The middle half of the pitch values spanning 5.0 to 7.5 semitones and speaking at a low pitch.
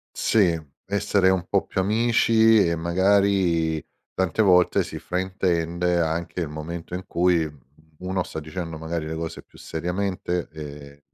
No: narrow, 2.5 semitones; very low, 90 Hz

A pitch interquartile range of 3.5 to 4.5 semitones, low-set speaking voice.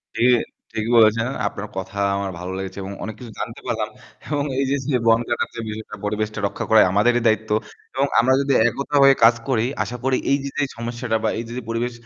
No: average, 2.7 semitones; low, 115 Hz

